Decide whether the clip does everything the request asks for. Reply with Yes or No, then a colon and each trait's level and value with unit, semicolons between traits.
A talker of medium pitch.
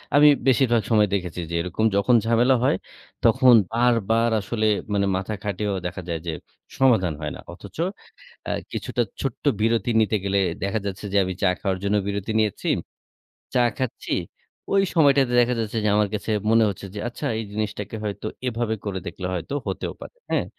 No: low, 110 Hz